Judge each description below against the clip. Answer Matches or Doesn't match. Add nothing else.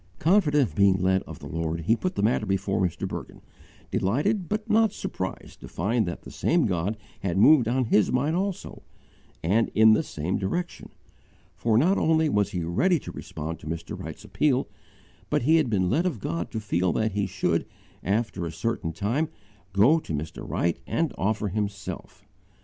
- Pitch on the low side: Matches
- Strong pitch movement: Matches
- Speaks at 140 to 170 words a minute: Doesn't match